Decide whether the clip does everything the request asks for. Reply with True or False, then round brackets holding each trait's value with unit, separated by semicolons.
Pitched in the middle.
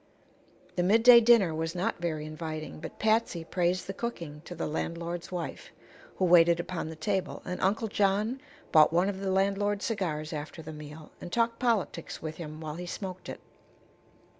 True (175 Hz)